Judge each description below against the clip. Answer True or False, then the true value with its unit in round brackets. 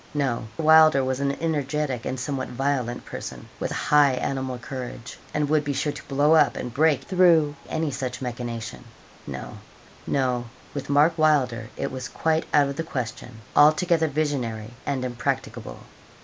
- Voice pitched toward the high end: False (140 Hz)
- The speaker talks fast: False (155 wpm)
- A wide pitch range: False (3.3 semitones)